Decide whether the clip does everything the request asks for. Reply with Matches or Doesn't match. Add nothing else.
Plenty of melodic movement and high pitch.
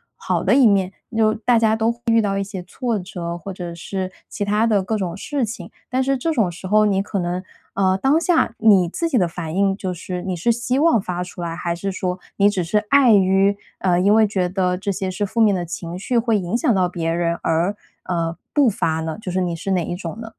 Doesn't match